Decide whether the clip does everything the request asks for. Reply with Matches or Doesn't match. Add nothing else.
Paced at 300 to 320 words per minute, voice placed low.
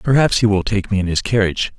Doesn't match